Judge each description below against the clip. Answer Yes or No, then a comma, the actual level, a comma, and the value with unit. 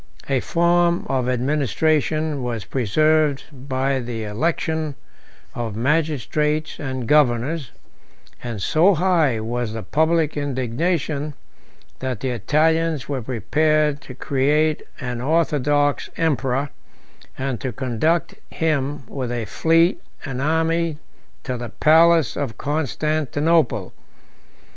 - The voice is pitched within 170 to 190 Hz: No, medium, 145 Hz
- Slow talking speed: Yes, slow, 110 wpm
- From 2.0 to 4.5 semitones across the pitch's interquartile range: Yes, average, 3.8 semitones